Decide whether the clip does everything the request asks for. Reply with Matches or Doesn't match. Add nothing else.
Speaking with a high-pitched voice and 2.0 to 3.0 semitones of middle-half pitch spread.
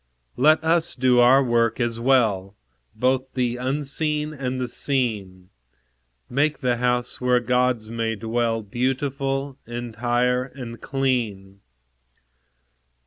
Doesn't match